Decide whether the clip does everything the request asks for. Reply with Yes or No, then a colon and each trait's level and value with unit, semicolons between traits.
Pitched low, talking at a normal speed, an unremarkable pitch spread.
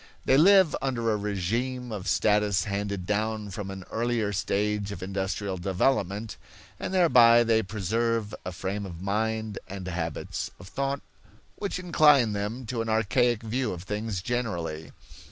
Yes: low, 105 Hz; average, 150 wpm; average, 3.4 semitones